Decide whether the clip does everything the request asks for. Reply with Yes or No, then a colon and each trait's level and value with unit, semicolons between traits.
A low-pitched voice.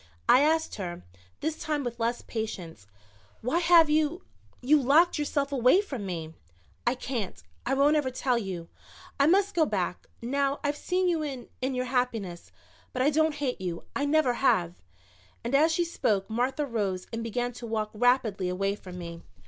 No: very high, 255 Hz